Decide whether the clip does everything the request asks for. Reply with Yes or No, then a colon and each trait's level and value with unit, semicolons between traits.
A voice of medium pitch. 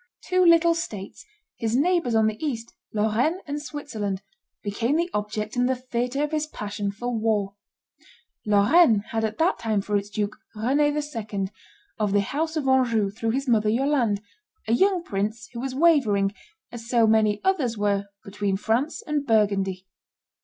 No: high, 225 Hz